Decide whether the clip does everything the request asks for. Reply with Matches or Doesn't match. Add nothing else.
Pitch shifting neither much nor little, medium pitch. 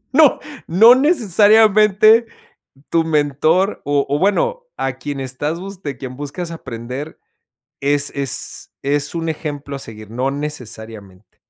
Doesn't match